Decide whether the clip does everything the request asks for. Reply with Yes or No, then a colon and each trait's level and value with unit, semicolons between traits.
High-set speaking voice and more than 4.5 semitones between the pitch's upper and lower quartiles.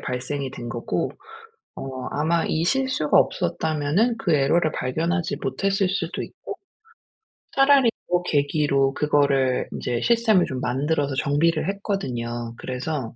No: medium, 150 Hz; average, 5.1 semitones